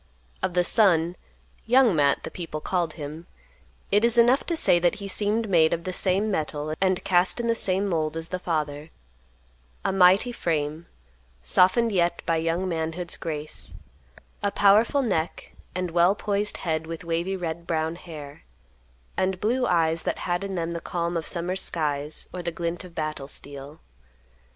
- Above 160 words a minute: Yes, average, 170 wpm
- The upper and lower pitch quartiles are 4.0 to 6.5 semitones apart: No, average, 3.2 semitones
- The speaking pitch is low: No, medium, 175 Hz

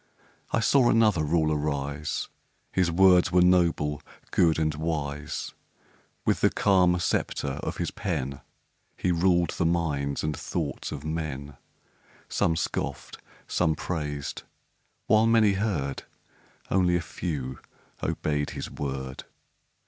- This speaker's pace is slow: Yes, slow, 120 wpm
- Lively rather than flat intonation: No, average, 3.7 semitones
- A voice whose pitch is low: Yes, very low, 80 Hz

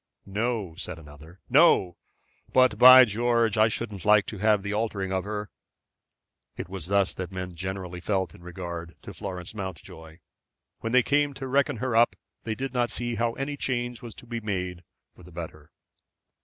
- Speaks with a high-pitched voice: No, low, 105 Hz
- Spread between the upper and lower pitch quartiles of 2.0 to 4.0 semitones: No, average, 4.7 semitones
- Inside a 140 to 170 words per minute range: No, average, 180 wpm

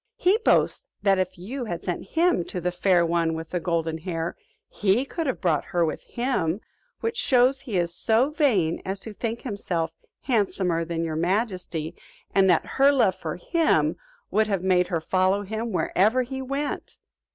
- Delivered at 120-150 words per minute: No, average, 180 wpm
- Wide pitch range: Yes, wide, 6.1 semitones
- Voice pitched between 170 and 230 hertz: Yes, high, 190 Hz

